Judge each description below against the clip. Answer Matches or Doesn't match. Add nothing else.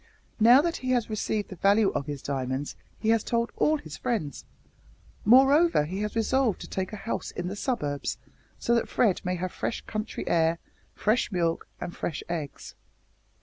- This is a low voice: Doesn't match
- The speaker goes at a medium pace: Matches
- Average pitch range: Doesn't match